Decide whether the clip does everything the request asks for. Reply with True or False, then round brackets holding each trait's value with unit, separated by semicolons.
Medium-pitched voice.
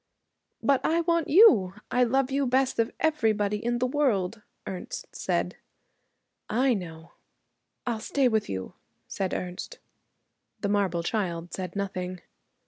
False (220 Hz)